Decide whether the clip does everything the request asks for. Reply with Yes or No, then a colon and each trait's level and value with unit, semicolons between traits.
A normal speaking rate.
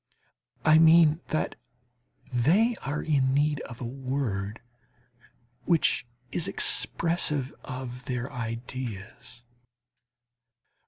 No: slow, 90 wpm